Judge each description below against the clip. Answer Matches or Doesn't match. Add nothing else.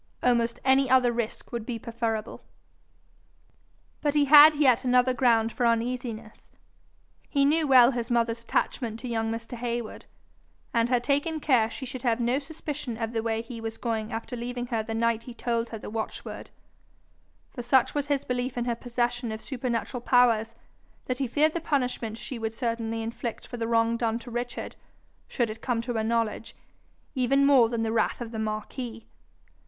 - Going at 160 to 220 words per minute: Matches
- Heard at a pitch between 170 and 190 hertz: Doesn't match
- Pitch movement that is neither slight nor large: Doesn't match